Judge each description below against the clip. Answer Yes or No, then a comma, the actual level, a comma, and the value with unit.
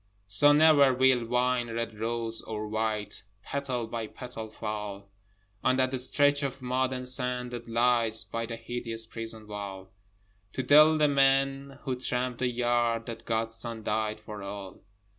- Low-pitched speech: Yes, low, 120 Hz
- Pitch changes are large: No, average, 2.7 semitones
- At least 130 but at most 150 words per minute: No, average, 160 wpm